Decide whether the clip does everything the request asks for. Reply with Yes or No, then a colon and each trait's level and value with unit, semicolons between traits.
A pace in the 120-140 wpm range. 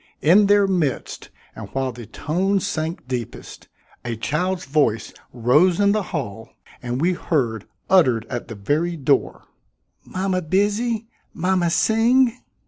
Yes: slow, 135 wpm